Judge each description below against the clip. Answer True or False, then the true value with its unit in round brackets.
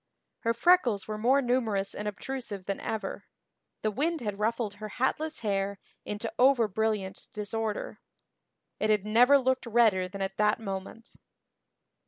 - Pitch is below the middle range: False (215 Hz)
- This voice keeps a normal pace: True (145 wpm)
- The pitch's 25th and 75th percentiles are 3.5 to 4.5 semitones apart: False (3.1 semitones)